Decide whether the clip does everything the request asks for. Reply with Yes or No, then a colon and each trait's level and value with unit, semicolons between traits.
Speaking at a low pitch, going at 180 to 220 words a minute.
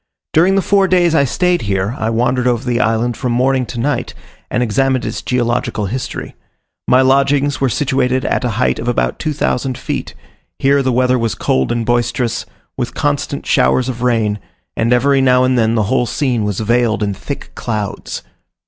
Yes: low, 125 Hz; average, 185 wpm